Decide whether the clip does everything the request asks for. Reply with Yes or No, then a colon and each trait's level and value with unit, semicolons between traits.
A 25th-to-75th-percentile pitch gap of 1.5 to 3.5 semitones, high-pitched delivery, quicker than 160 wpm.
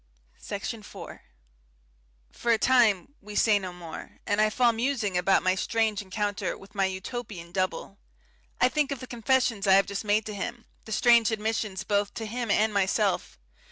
Yes: average, 3.0 semitones; high, 210 Hz; average, 175 wpm